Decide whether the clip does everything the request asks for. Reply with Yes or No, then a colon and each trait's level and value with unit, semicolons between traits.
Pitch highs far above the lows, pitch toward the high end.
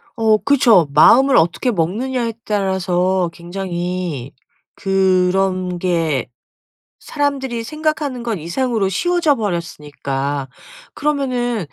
Yes: wide, 6.2 semitones; high, 195 Hz